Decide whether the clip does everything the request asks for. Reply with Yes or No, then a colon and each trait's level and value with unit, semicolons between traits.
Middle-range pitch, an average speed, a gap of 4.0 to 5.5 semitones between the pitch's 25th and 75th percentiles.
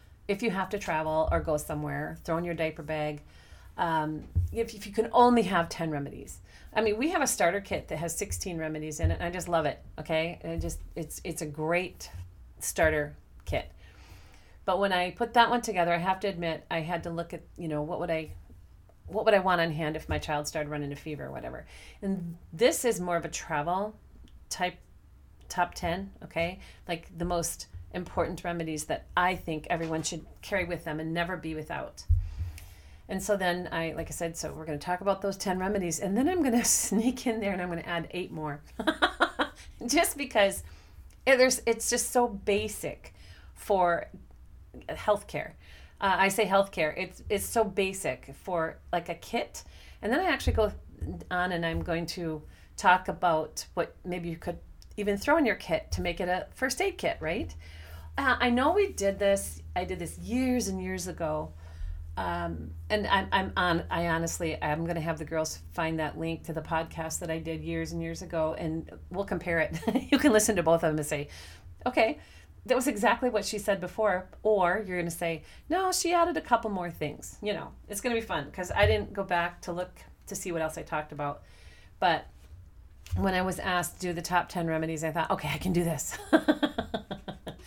No: medium, 170 Hz; fast, 210 wpm; average, 4.7 semitones